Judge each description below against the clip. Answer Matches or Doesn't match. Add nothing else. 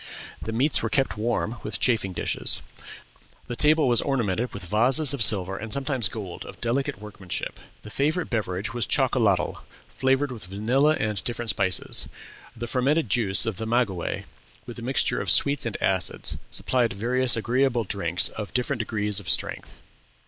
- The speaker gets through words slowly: Doesn't match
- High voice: Doesn't match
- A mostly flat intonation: Doesn't match